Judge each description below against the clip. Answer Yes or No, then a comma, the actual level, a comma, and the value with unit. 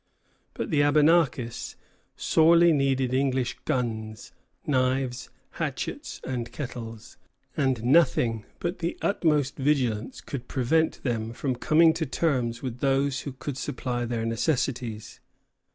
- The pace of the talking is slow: Yes, slow, 120 wpm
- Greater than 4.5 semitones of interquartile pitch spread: No, average, 3.4 semitones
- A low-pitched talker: Yes, low, 130 Hz